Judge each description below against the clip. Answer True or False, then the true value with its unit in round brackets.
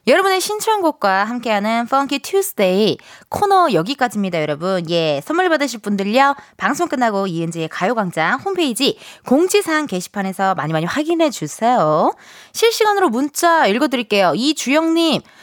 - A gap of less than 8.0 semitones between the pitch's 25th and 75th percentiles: False (8.7 semitones)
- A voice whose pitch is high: True (250 Hz)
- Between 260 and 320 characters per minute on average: False (360 characters per minute)